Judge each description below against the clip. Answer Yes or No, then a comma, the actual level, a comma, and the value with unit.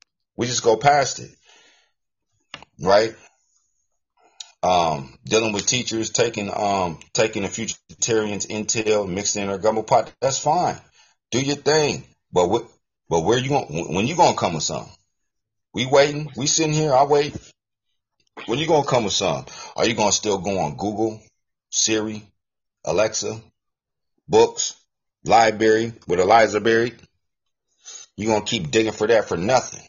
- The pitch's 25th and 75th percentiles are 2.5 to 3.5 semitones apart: Yes, average, 2.9 semitones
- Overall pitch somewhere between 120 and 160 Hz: No, low, 110 Hz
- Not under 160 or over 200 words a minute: No, average, 150 wpm